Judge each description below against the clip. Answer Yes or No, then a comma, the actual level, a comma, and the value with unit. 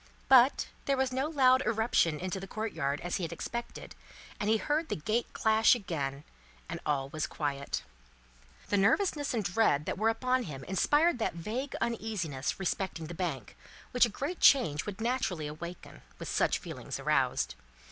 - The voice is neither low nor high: No, high, 210 Hz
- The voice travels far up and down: Yes, wide, 7.4 semitones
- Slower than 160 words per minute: No, average, 165 wpm